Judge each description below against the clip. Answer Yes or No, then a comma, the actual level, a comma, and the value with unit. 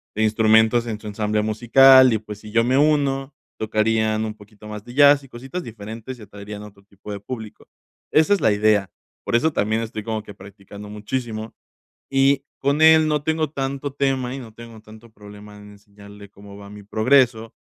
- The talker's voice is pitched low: Yes, low, 110 Hz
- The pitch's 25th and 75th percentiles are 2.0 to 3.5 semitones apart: No, average, 4.1 semitones